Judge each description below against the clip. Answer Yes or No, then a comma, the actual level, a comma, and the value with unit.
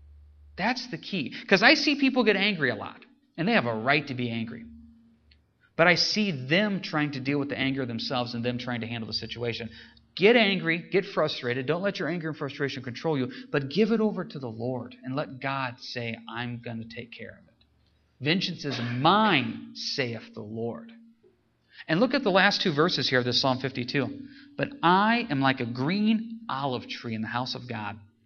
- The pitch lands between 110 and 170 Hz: Yes, low, 135 Hz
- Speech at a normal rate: No, fast, 210 wpm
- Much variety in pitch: Yes, wide, 8.4 semitones